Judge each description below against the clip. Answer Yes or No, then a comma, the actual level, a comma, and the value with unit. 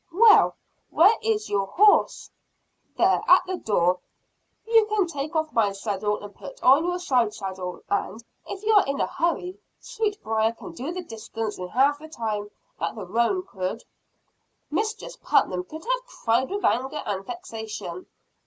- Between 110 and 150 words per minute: No, average, 160 wpm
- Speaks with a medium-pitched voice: No, very high, 275 Hz